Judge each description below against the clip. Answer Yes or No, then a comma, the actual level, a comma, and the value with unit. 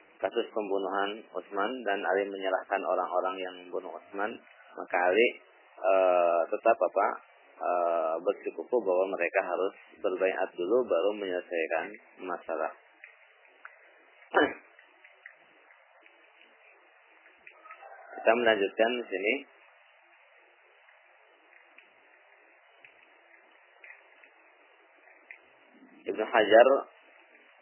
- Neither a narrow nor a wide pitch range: Yes, average, 3.5 semitones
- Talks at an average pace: No, slow, 65 wpm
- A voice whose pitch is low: Yes, low, 100 Hz